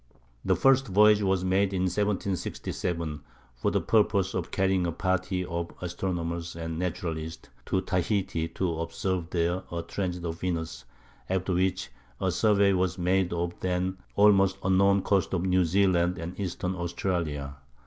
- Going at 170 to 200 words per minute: No, average, 150 wpm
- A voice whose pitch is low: Yes, very low, 90 Hz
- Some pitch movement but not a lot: No, narrow, 2.1 semitones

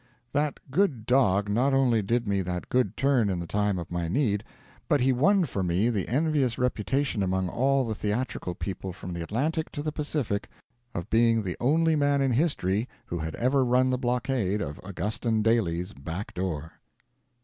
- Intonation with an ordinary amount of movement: No, wide, 6.1 semitones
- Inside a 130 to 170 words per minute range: No, average, 180 wpm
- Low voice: Yes, low, 115 Hz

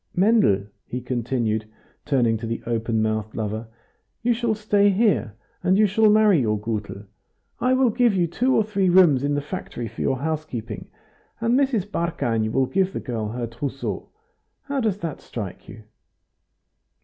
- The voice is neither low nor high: Yes, medium, 145 Hz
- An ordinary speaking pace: Yes, average, 165 wpm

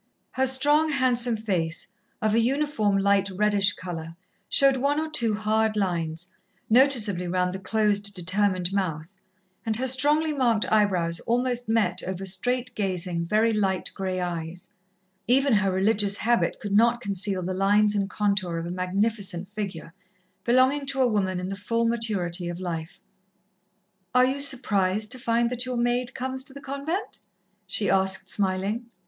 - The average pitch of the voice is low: No, high, 210 Hz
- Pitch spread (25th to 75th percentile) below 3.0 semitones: No, average, 4.7 semitones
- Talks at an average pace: Yes, average, 155 wpm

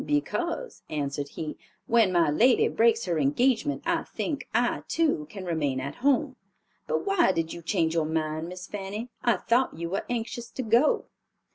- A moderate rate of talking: Yes, average, 170 wpm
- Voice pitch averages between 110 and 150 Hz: No, high, 200 Hz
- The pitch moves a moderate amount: No, wide, 7.3 semitones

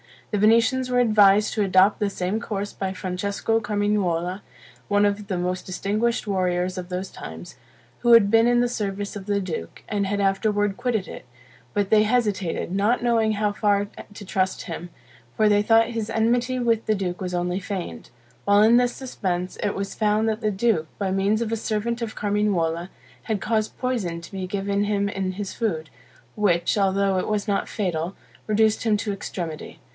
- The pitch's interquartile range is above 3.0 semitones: No, average, 2.7 semitones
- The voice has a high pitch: Yes, high, 205 Hz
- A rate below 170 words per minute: No, average, 185 wpm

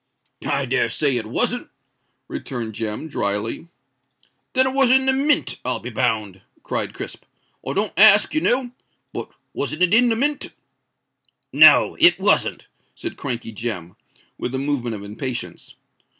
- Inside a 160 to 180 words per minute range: No, average, 145 wpm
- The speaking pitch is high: No, medium, 140 Hz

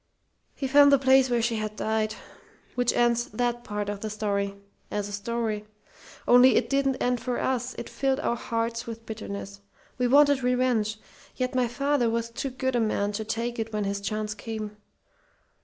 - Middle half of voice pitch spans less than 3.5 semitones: Yes, average, 2.9 semitones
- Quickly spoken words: No, average, 190 wpm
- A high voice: Yes, high, 230 Hz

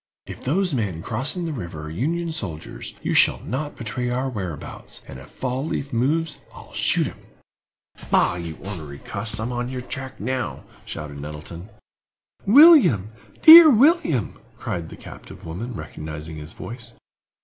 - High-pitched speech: No, low, 120 Hz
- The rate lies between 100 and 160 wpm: Yes, average, 150 wpm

